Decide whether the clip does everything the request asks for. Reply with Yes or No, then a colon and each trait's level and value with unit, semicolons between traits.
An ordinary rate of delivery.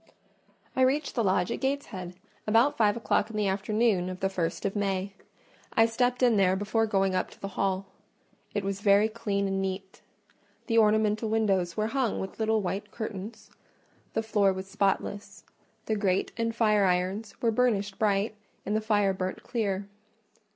Yes: average, 170 wpm